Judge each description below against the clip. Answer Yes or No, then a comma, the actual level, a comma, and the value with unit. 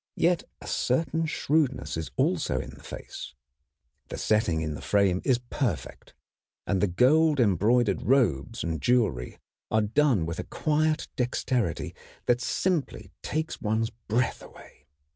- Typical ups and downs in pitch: No, wide, 6.6 semitones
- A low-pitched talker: Yes, low, 120 Hz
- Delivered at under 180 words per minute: Yes, average, 140 wpm